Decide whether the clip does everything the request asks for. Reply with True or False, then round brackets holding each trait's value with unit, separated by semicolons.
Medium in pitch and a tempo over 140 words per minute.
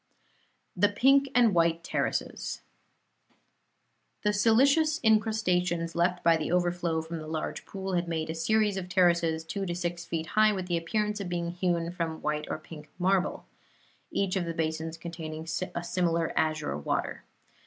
True (175 Hz; 160 wpm)